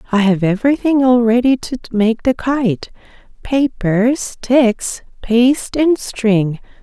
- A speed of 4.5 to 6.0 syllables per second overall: No, 3.6 syllables/s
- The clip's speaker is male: No, female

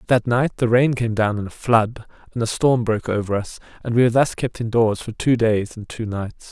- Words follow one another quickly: Yes, fast, 260 wpm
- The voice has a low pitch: Yes, low, 115 Hz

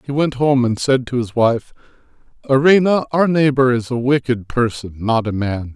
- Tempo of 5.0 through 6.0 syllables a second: No, 4.8 syllables/s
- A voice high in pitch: No, low, 125 Hz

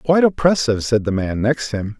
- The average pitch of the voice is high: No, low, 125 Hz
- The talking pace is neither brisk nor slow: No, fast, 210 wpm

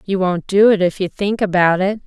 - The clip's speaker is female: Yes, female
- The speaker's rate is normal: No, fast, 260 wpm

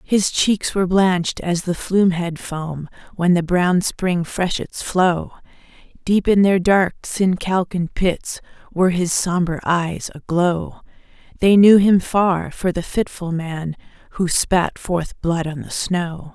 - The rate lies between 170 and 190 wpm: No, average, 155 wpm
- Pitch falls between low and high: Yes, medium, 180 Hz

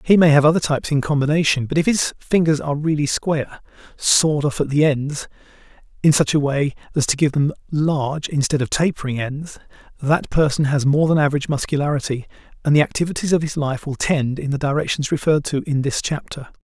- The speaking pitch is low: No, medium, 145 Hz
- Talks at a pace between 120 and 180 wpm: No, average, 190 wpm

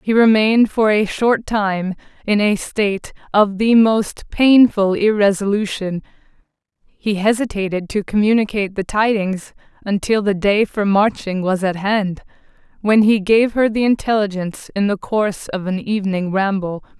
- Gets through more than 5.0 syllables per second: No, 4.6 syllables/s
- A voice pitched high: Yes, high, 205 Hz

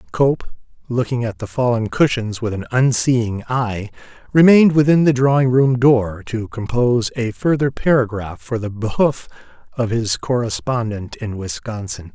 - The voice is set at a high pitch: No, low, 120 Hz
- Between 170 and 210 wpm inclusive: No, average, 145 wpm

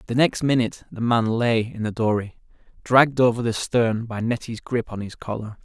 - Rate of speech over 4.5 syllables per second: Yes, 5.3 syllables/s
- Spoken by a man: Yes, male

